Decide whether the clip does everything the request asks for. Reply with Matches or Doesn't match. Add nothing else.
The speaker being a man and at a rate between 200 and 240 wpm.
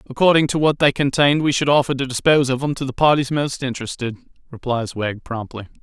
Matches